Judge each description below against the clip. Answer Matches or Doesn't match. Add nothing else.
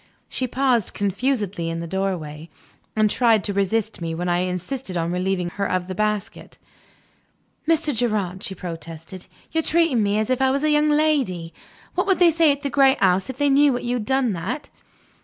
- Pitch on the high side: Matches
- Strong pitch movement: Matches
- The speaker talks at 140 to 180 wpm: Doesn't match